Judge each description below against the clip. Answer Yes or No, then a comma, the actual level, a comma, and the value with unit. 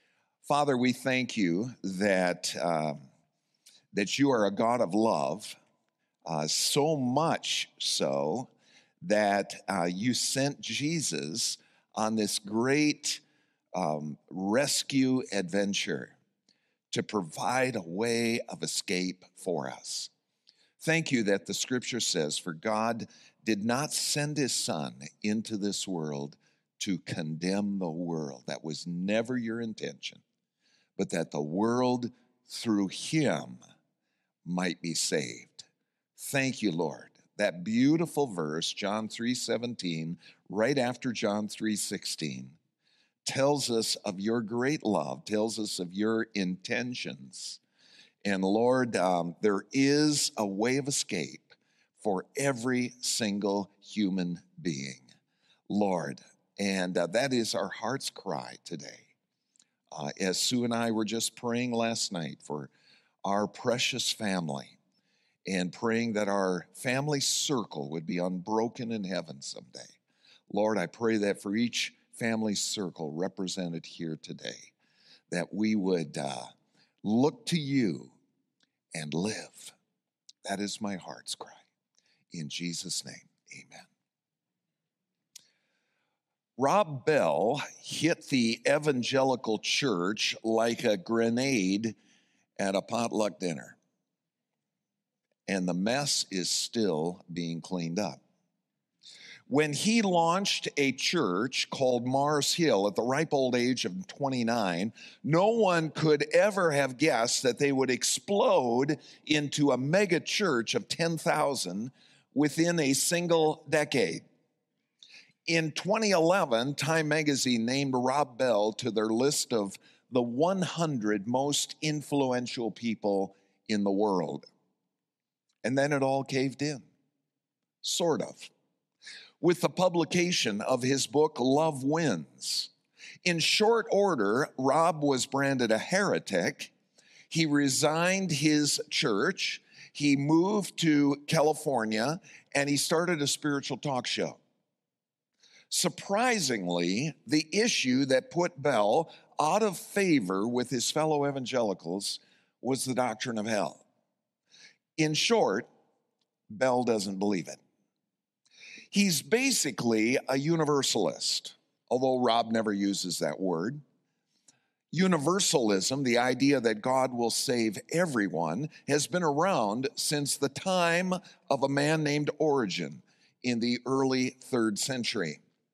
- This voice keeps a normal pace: No, slow, 115 wpm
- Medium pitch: No, low, 125 Hz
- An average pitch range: No, wide, 6.4 semitones